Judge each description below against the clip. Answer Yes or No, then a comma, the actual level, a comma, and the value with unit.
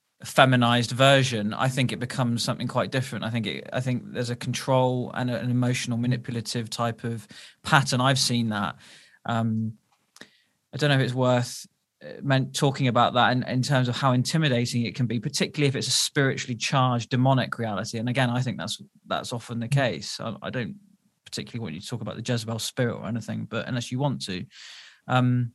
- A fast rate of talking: No, average, 195 wpm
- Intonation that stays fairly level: Yes, narrow, 2.0 semitones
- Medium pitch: No, low, 125 Hz